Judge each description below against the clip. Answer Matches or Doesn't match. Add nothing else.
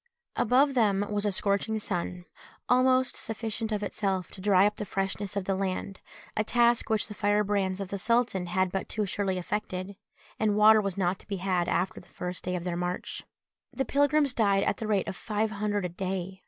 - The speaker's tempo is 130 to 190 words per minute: Doesn't match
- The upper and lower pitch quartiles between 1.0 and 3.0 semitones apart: Matches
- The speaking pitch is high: Matches